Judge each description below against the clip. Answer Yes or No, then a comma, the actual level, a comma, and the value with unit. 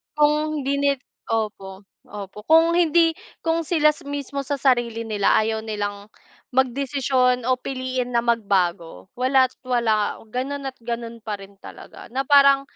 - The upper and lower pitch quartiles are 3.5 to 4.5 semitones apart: Yes, average, 4.2 semitones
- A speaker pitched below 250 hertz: No, very high, 255 Hz